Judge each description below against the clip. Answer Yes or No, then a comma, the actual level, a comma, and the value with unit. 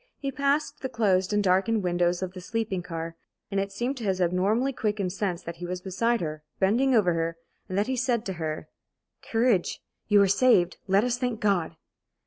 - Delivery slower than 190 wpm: No, average, 200 wpm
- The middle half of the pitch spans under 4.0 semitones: No, average, 4.7 semitones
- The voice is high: Yes, high, 195 Hz